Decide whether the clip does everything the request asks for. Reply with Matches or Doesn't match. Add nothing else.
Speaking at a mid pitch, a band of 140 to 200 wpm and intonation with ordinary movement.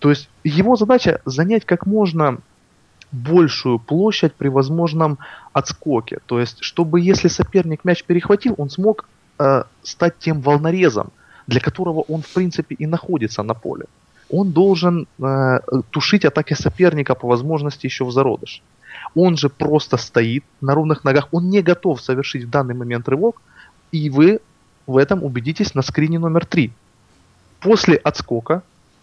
Matches